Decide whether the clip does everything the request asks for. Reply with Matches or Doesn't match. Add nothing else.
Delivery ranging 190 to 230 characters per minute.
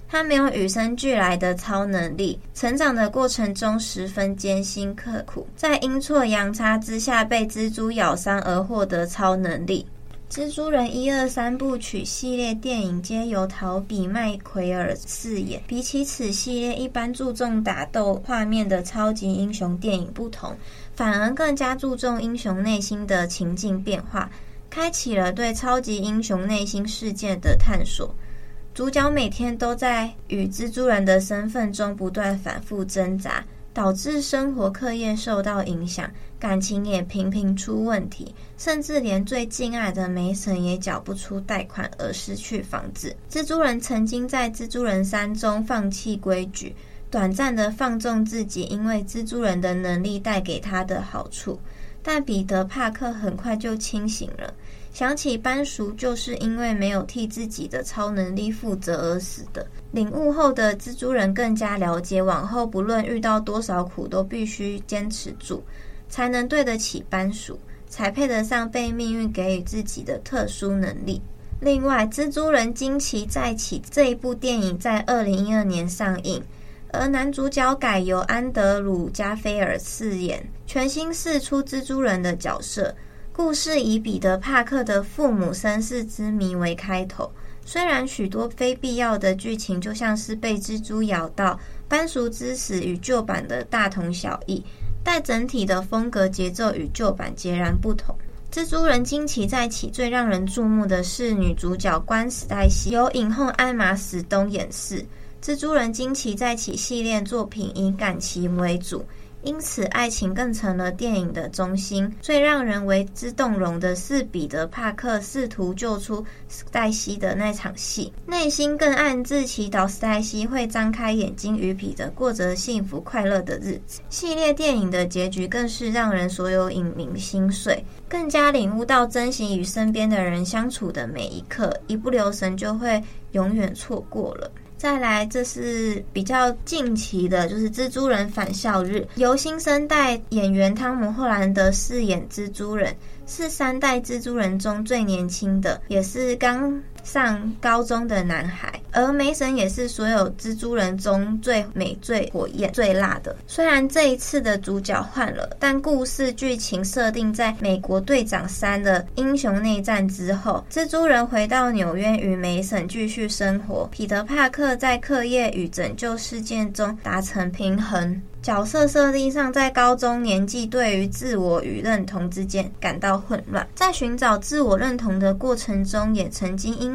Doesn't match